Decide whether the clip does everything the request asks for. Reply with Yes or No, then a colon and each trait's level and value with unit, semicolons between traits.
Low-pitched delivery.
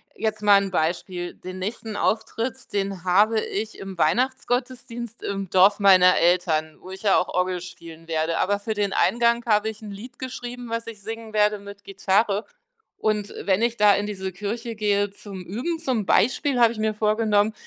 No: high, 205 Hz